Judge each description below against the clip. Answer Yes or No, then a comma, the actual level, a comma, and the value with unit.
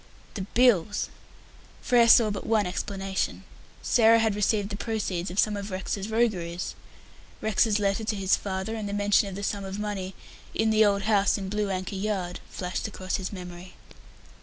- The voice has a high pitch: Yes, high, 200 Hz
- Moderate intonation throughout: No, narrow, 2.2 semitones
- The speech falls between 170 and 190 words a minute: Yes, average, 175 wpm